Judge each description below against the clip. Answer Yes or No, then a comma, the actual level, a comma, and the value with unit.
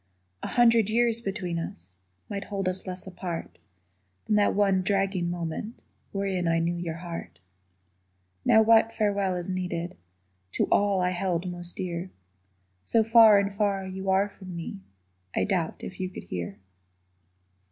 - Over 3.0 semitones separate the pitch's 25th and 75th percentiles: No, average, 2.7 semitones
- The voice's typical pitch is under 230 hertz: Yes, high, 190 Hz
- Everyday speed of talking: Yes, average, 150 wpm